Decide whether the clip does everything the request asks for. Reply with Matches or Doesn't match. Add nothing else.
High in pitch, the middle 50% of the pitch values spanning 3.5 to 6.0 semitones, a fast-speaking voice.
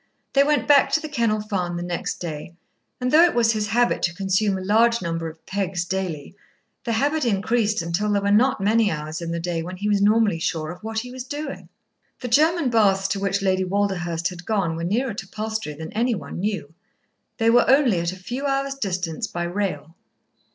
Matches